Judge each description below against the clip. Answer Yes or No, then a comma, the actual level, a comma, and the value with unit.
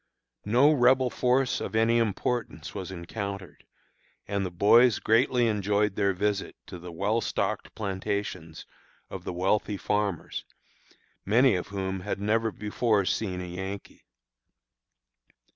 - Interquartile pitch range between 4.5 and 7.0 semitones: No, average, 3.0 semitones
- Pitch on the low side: Yes, low, 105 Hz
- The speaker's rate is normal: No, slow, 125 wpm